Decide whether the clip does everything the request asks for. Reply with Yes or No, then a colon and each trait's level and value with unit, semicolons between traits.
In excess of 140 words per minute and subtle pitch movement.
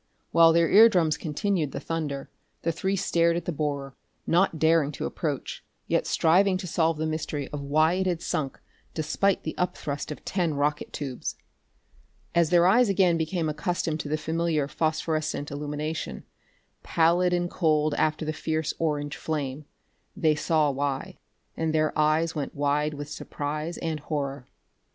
Yes: average, 160 wpm; narrow, 2.3 semitones